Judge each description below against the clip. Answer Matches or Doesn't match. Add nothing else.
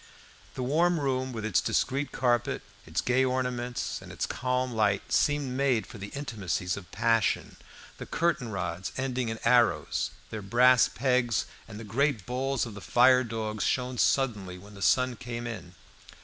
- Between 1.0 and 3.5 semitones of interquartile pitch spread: Matches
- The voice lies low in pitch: Matches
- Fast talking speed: Doesn't match